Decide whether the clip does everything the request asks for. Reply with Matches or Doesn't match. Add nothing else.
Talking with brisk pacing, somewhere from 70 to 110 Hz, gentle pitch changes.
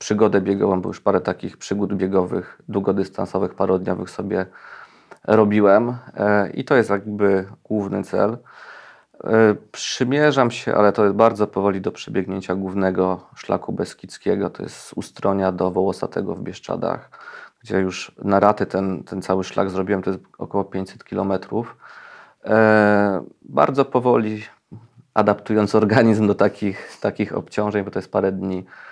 Doesn't match